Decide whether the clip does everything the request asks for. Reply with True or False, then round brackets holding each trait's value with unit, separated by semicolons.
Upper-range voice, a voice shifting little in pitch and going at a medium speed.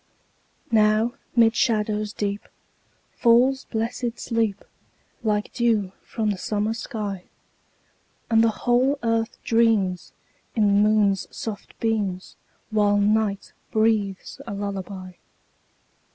False (215 Hz; 2.0 semitones; 105 wpm)